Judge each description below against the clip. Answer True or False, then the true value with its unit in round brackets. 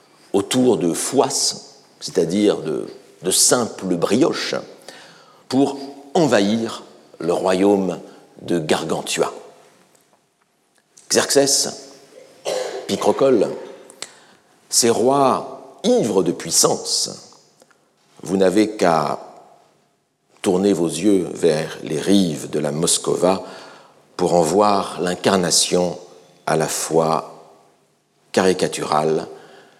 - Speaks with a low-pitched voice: True (105 Hz)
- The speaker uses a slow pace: True (85 wpm)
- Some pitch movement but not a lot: False (7.7 semitones)